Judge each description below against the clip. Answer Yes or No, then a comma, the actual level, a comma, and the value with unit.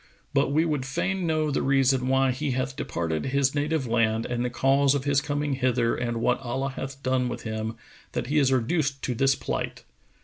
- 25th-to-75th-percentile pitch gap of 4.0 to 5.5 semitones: No, narrow, 2.4 semitones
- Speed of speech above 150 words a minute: Yes, fast, 205 wpm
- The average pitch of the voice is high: No, low, 135 Hz